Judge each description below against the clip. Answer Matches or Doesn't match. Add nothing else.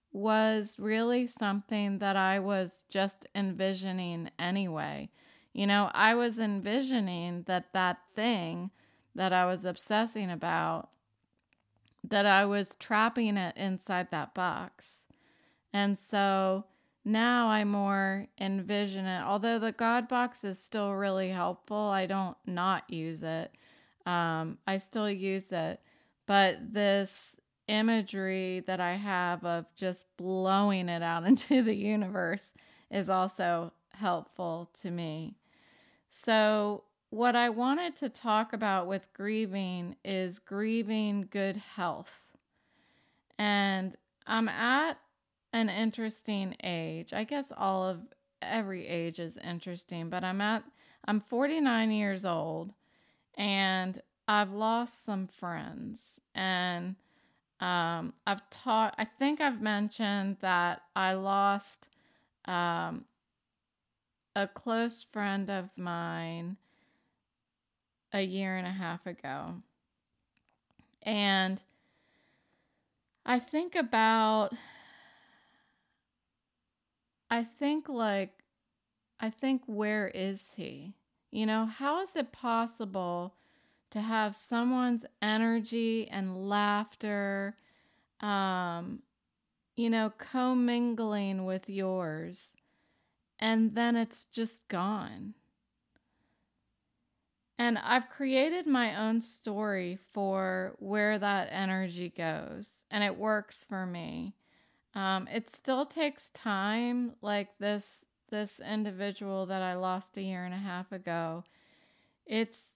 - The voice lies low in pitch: Doesn't match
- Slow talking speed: Matches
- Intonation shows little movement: Doesn't match